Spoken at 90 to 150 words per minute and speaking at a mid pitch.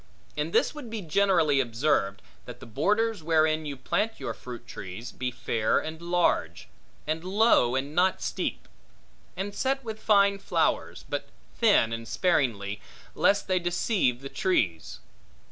Yes: average, 145 wpm; medium, 160 Hz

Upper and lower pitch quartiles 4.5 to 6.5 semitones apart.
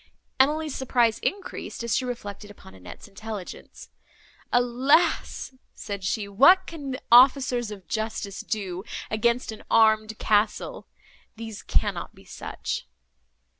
No: average, 3.9 semitones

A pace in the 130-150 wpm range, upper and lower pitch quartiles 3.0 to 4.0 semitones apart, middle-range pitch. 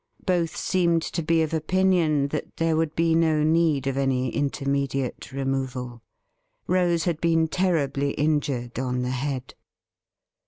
Yes: slow, 135 wpm; average, 3.4 semitones; medium, 150 Hz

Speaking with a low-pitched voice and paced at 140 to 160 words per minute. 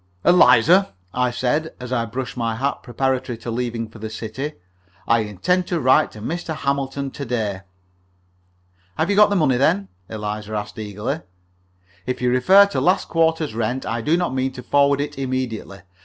No: low, 125 Hz; average, 175 wpm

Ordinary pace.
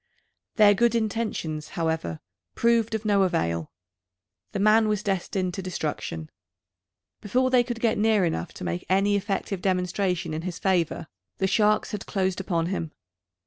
Yes: average, 150 wpm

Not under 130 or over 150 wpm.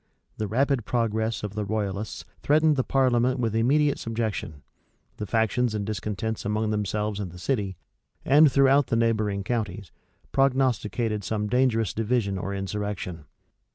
Yes: average, 140 wpm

